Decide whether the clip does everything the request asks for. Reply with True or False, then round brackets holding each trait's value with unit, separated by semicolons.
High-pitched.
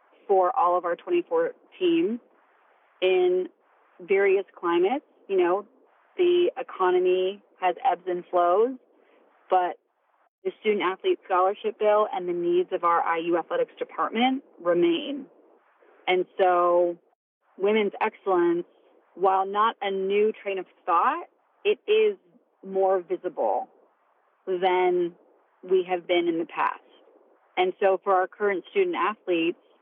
True (220 Hz)